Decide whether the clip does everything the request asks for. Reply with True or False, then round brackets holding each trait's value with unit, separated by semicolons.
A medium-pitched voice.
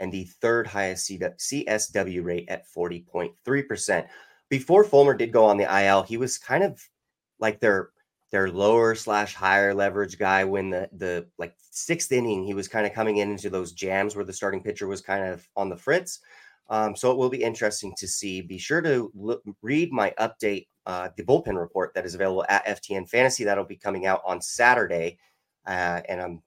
False (100 Hz)